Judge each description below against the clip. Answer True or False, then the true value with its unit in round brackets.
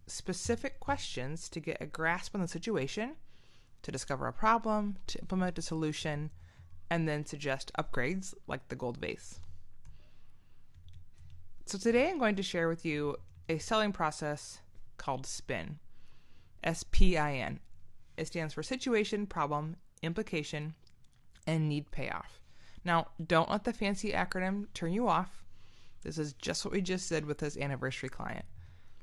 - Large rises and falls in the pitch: True (7.8 semitones)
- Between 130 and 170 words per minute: True (145 wpm)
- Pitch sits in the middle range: True (155 Hz)